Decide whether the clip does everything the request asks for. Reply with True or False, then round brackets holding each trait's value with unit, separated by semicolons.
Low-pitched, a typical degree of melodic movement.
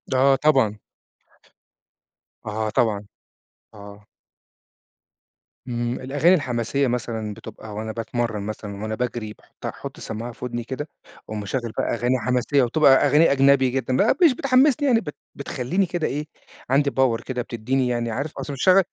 True (125 Hz; 3.9 semitones)